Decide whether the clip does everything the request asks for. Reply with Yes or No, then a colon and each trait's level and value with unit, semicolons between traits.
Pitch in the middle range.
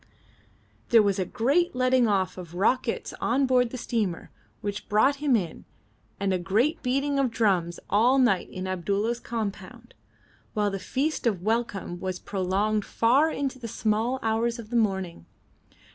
No: high, 220 Hz